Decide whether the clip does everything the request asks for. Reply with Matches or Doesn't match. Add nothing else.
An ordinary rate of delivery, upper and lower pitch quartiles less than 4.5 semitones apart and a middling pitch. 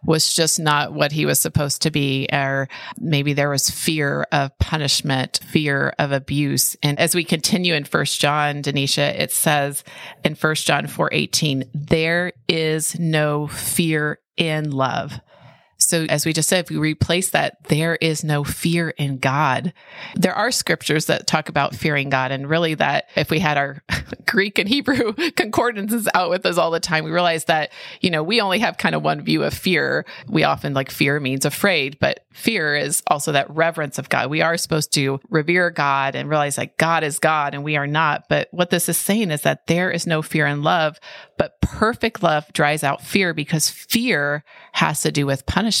Matches